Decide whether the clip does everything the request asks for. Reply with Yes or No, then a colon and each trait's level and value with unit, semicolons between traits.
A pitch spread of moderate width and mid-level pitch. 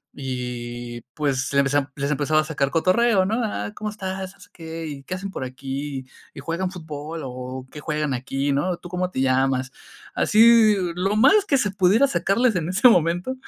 No: wide, 5.9 semitones; medium, 160 Hz